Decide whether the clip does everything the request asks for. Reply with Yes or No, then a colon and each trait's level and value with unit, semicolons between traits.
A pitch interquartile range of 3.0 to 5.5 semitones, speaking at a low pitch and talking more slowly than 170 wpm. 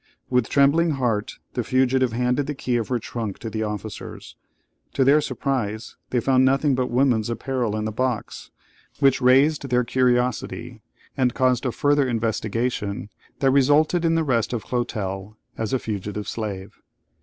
Yes: average, 3.4 semitones; low, 125 Hz; average, 160 wpm